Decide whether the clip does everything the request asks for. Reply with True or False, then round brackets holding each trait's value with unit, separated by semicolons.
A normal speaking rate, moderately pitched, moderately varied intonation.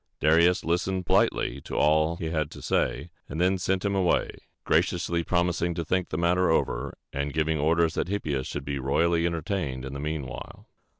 False (185 wpm; 85 Hz; 3.0 semitones)